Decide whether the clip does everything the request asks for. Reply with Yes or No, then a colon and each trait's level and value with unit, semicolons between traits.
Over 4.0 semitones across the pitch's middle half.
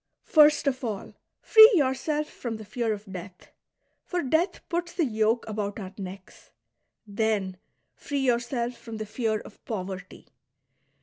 Yes: average, 5.1 semitones